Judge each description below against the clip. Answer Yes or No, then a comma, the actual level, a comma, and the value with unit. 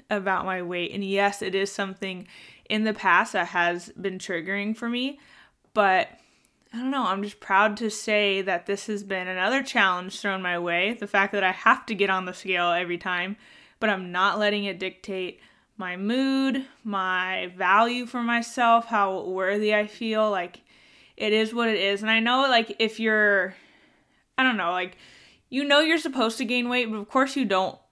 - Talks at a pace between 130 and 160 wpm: No, average, 195 wpm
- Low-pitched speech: No, high, 205 Hz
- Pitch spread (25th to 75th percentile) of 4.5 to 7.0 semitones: No, average, 3.6 semitones